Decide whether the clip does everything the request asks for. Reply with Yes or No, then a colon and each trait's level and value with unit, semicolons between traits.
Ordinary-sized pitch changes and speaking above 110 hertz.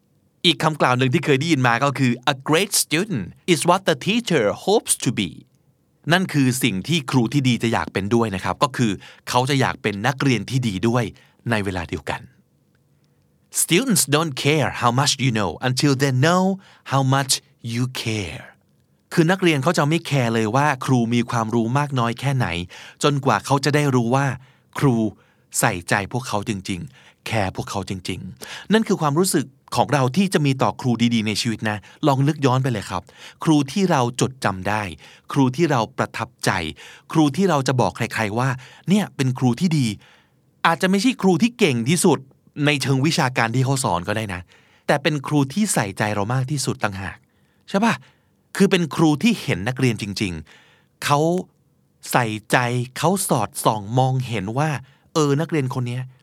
Yes: average, 5.0 semitones; low, 130 Hz